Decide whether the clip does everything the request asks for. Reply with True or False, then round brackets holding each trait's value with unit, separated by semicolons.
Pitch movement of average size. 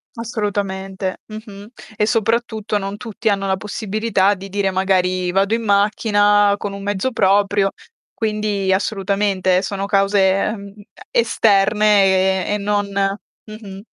False (1.5 semitones)